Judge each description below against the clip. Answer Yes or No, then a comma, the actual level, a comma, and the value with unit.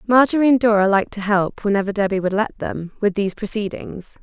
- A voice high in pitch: Yes, high, 205 Hz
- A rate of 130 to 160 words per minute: No, average, 200 wpm